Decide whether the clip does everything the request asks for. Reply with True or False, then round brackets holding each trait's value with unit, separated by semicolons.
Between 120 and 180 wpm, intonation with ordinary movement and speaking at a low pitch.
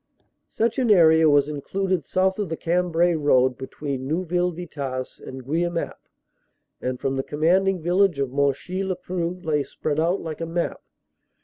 False (170 wpm; 4.1 semitones; 165 Hz)